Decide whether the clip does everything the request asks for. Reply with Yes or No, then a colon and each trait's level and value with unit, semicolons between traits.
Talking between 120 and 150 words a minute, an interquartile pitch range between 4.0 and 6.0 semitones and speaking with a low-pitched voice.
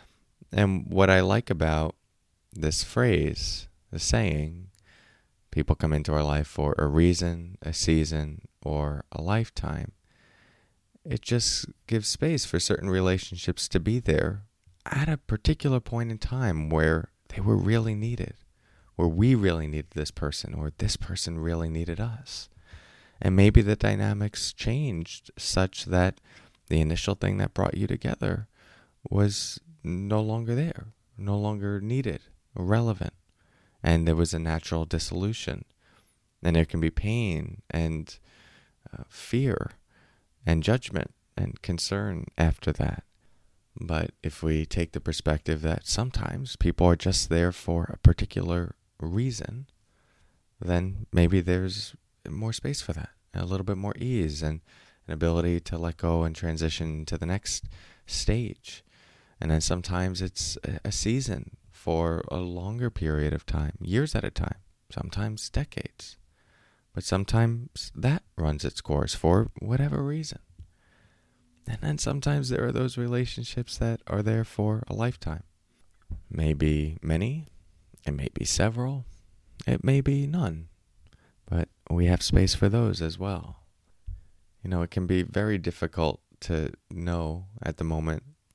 Yes: average, 140 wpm; average, 5.3 semitones; very low, 95 Hz